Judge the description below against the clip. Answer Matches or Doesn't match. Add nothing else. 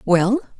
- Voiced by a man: Doesn't match